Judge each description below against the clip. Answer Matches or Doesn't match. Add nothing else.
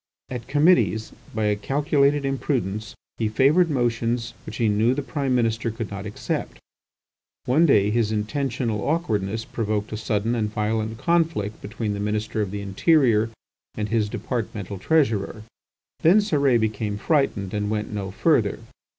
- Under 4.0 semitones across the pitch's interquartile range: Doesn't match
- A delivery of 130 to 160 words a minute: Matches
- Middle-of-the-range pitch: Doesn't match